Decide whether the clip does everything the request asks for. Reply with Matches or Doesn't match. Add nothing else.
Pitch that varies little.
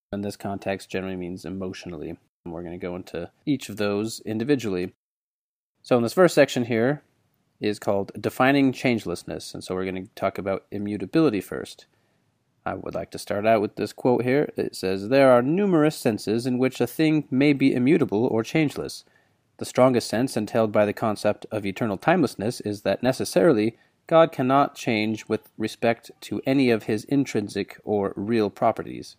Doesn't match